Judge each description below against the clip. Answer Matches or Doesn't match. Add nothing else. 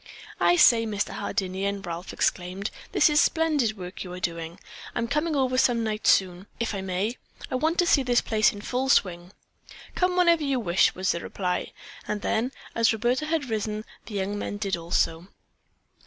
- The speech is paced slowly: Doesn't match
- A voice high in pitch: Matches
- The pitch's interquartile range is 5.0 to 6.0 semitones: Matches